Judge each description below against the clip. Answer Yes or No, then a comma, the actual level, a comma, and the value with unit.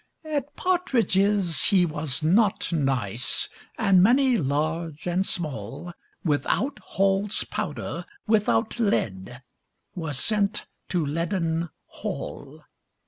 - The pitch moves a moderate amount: No, wide, 5.8 semitones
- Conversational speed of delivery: No, slow, 95 wpm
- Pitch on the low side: No, medium, 175 Hz